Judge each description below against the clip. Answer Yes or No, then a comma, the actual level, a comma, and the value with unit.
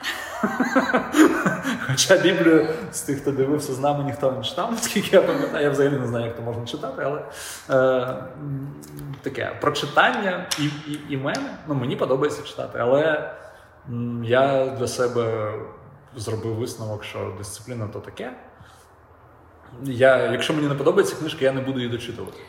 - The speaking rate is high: No, average, 145 wpm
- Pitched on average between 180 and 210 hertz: No, low, 130 Hz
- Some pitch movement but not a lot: Yes, average, 4.1 semitones